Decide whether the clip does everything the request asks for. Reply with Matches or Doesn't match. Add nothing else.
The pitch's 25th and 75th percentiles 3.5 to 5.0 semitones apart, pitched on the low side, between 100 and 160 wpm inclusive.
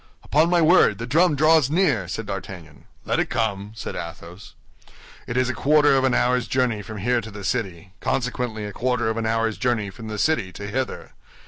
Doesn't match